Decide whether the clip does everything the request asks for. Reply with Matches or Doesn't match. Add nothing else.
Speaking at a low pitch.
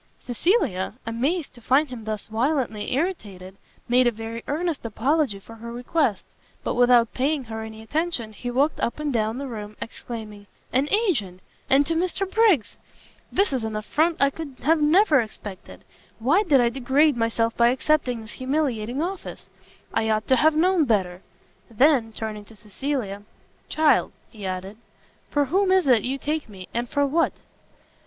Doesn't match